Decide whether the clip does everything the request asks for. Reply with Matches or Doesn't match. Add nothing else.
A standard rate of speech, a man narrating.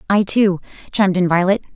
Doesn't match